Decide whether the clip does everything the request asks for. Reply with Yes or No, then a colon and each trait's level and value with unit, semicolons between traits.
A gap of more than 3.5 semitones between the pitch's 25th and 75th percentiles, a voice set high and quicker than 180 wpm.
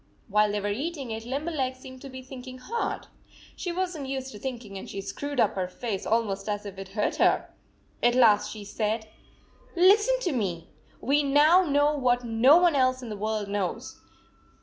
Yes: wide, 5.4 semitones; very high, 250 Hz; average, 200 wpm